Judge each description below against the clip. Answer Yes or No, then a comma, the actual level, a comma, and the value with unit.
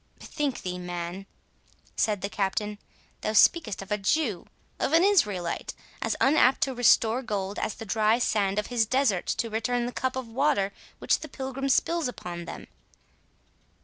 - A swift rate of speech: No, average, 155 wpm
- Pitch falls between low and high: No, high, 220 Hz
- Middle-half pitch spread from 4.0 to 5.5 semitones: Yes, average, 5.0 semitones